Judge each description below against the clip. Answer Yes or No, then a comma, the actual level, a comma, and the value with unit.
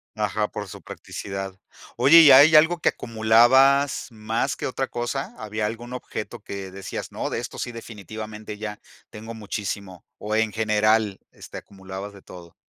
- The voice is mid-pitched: No, low, 110 Hz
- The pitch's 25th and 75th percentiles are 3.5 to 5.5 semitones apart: No, average, 2.7 semitones